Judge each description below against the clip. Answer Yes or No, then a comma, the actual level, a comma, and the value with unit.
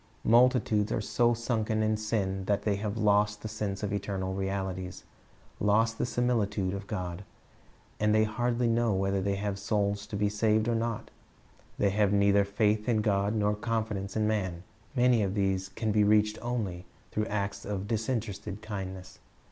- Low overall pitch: Yes, low, 105 Hz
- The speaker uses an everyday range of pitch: No, narrow, 1.9 semitones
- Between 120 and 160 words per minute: No, average, 170 wpm